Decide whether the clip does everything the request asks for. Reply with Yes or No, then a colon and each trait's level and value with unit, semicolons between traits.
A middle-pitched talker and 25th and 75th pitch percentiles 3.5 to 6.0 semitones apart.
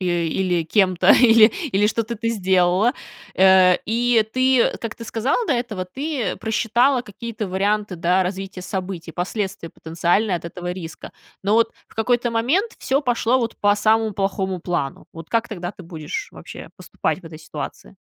No: high, 205 Hz; average, 4.2 semitones